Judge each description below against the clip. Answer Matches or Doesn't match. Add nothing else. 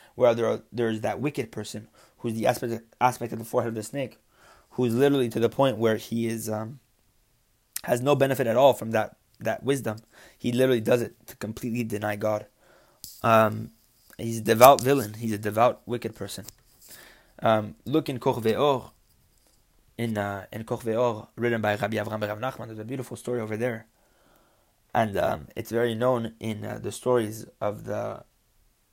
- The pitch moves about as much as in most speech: Doesn't match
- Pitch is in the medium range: Doesn't match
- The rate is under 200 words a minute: Matches